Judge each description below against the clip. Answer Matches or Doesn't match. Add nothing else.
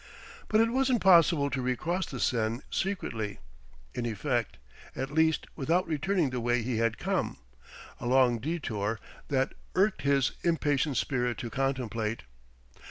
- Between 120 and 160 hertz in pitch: Matches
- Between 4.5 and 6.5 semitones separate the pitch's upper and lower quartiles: Matches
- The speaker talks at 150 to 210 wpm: Doesn't match